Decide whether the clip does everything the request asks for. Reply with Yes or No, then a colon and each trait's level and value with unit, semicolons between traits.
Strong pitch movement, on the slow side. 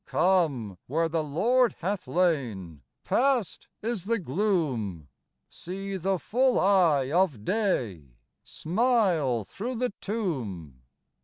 Yes: wide, 8.5 semitones; slow, 105 wpm